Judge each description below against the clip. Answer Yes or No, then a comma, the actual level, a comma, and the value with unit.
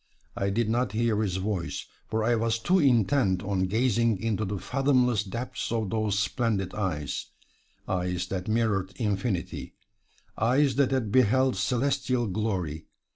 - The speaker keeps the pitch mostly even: No, average, 3.8 semitones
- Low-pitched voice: Yes, low, 110 Hz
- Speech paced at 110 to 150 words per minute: Yes, average, 140 wpm